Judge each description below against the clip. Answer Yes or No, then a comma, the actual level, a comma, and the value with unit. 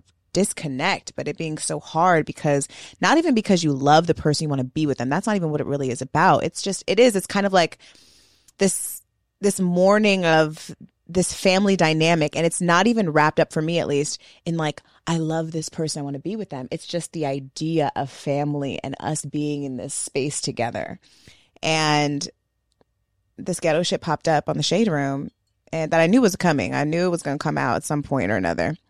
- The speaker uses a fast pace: Yes, fast, 220 wpm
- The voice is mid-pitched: Yes, medium, 155 Hz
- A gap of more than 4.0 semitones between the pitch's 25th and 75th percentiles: No, average, 3.7 semitones